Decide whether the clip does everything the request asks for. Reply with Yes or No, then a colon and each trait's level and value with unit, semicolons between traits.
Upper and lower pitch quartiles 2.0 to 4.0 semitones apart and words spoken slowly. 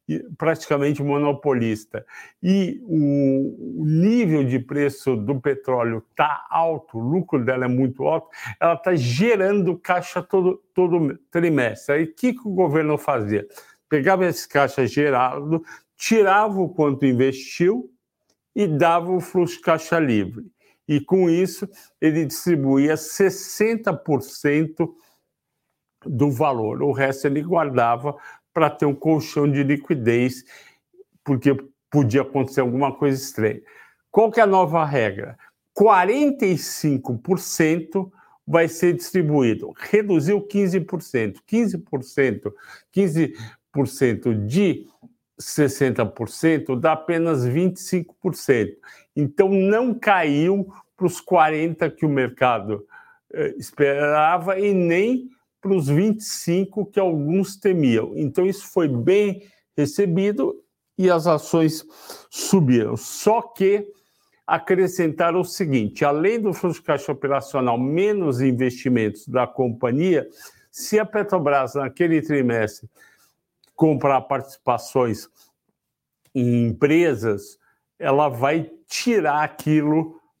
No: average, 5.3 semitones; slow, 105 wpm